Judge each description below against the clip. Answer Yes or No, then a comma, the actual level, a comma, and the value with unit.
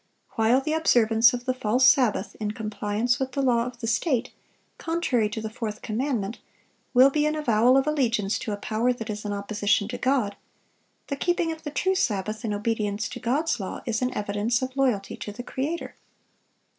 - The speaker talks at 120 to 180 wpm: No, average, 195 wpm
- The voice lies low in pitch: No, high, 235 Hz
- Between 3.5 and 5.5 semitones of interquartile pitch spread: Yes, average, 4.0 semitones